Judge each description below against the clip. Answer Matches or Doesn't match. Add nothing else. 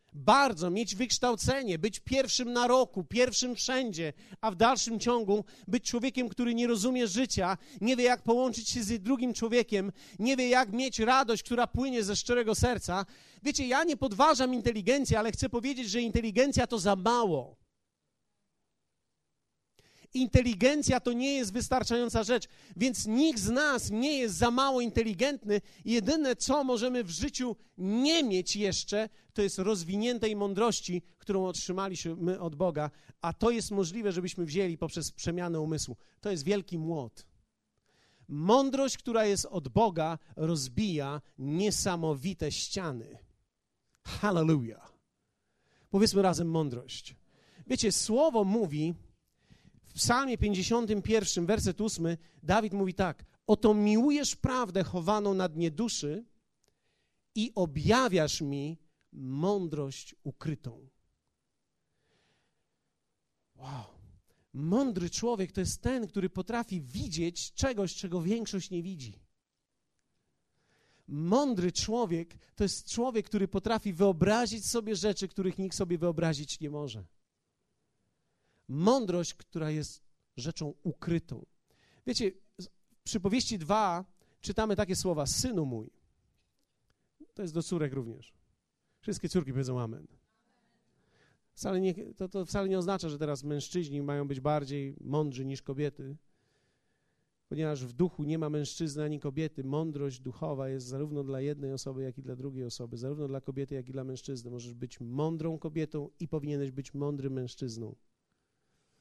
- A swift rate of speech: Doesn't match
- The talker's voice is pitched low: Doesn't match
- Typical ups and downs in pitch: Doesn't match